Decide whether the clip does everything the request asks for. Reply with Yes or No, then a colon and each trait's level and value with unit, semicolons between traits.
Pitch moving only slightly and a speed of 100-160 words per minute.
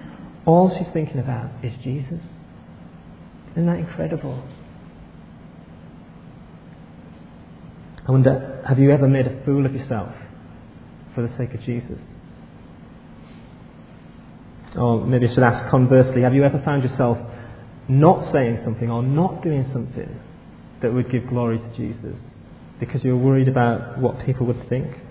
Yes: narrow, 2.3 semitones; slow, 135 wpm